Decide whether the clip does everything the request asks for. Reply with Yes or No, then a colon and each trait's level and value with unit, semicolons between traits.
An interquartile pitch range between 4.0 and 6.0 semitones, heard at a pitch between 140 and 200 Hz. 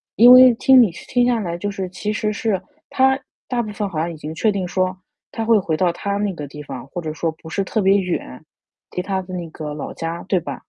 Yes: average, 4.6 semitones; high, 190 Hz